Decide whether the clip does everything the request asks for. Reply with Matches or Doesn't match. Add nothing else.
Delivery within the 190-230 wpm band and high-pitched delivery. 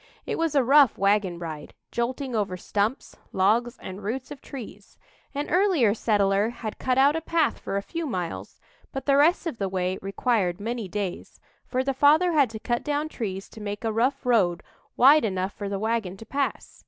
Matches